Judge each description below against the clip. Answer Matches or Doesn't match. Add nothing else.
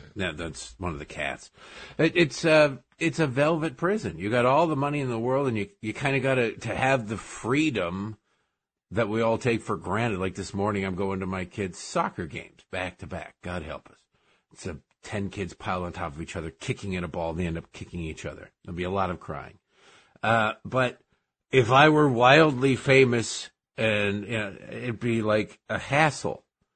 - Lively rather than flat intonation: Matches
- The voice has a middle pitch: Doesn't match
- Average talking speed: Doesn't match